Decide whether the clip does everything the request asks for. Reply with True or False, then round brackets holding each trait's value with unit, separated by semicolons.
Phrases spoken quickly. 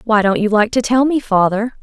True (265 wpm)